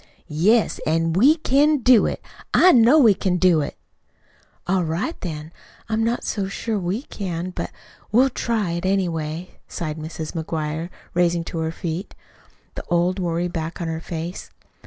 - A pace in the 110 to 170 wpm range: Yes, average, 160 wpm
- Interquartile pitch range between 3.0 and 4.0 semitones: No, average, 4.9 semitones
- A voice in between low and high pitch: Yes, medium, 175 Hz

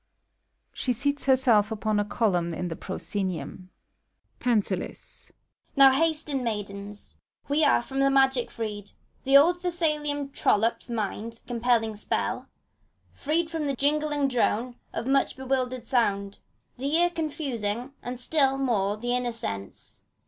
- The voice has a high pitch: Yes, very high, 250 Hz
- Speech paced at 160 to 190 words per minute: No, slow, 135 wpm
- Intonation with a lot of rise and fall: No, average, 4.9 semitones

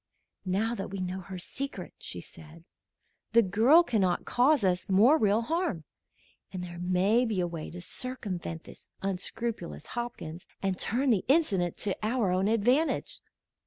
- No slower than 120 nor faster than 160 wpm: Yes, average, 155 wpm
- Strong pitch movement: No, average, 4.9 semitones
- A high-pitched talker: Yes, high, 200 Hz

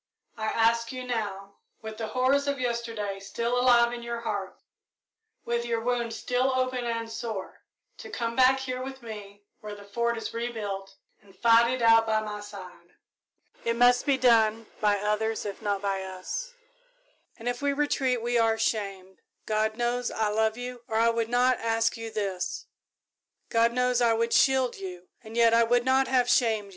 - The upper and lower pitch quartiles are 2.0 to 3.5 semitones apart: Yes, narrow, 2.4 semitones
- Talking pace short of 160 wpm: No, average, 185 wpm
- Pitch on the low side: No, high, 230 Hz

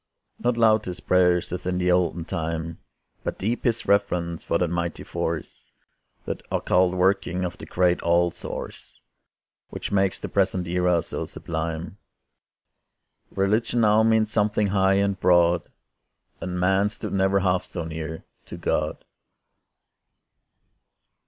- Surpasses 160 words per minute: No, slow, 135 wpm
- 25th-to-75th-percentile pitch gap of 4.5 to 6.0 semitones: No, narrow, 2.5 semitones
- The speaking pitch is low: Yes, very low, 90 Hz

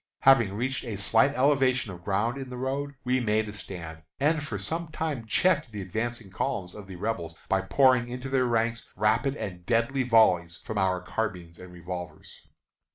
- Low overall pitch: Yes, low, 115 Hz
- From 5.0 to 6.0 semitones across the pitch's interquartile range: Yes, wide, 5.5 semitones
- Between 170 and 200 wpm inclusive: Yes, average, 180 wpm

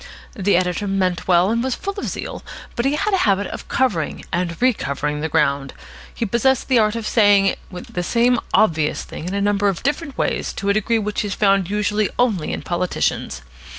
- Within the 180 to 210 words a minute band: Yes, average, 200 wpm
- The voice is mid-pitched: No, high, 200 Hz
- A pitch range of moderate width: Yes, average, 4.6 semitones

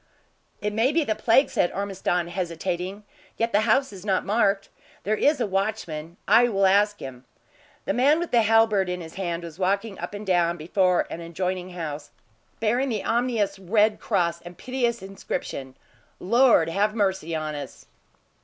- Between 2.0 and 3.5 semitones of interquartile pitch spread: No, average, 4.3 semitones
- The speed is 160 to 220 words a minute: Yes, average, 170 wpm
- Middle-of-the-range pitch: No, high, 195 Hz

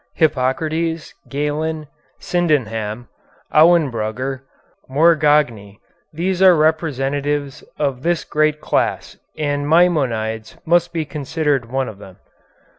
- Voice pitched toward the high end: No, medium, 145 Hz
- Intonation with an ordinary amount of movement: Yes, average, 3.6 semitones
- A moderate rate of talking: No, slow, 95 wpm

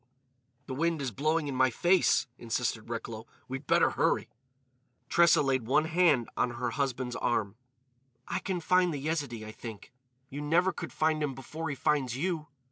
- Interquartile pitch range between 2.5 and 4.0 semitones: No, average, 4.6 semitones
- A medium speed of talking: Yes, average, 170 wpm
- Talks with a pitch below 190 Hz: Yes, medium, 140 Hz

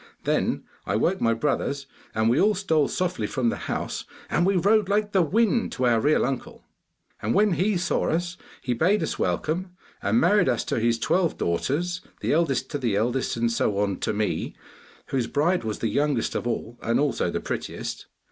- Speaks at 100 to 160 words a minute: No, average, 195 wpm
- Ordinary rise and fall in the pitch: No, wide, 7.6 semitones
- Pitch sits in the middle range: Yes, medium, 150 Hz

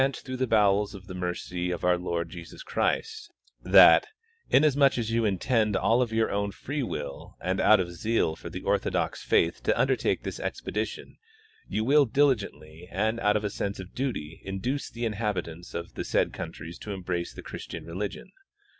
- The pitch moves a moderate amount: Yes, average, 4.6 semitones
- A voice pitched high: No, low, 105 Hz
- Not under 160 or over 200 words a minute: Yes, average, 180 wpm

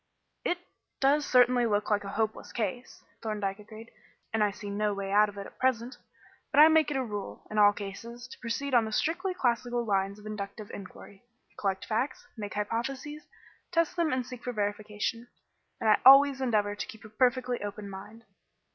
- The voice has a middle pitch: No, high, 225 Hz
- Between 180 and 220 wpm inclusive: Yes, average, 190 wpm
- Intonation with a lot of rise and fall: No, average, 3.7 semitones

